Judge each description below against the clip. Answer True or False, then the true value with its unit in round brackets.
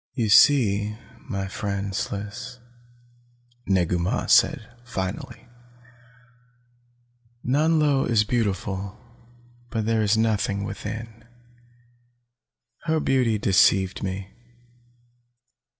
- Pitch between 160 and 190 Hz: False (105 Hz)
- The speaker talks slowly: True (80 wpm)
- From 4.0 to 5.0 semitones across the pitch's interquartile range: False (3.3 semitones)